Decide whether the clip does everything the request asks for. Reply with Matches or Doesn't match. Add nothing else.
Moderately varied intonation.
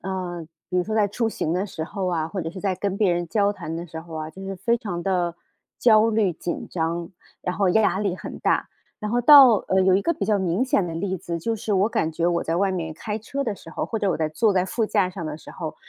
Matches